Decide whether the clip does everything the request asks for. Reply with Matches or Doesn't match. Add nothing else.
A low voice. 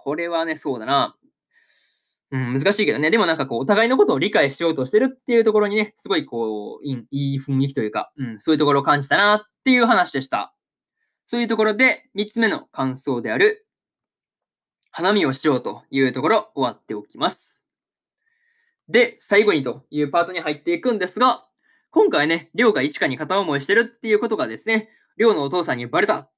Doesn't match